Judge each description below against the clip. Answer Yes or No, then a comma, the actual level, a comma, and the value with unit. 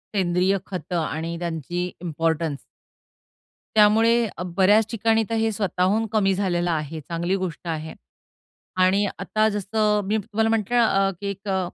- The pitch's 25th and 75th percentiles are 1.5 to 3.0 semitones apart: No, average, 3.6 semitones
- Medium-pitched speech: No, high, 195 Hz